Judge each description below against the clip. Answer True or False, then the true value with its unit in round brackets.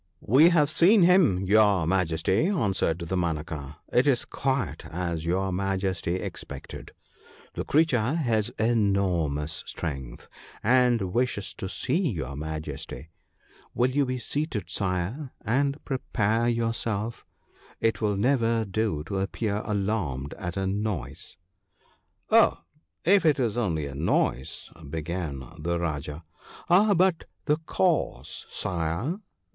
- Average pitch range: False (7.0 semitones)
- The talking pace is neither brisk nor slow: False (130 wpm)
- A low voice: True (100 Hz)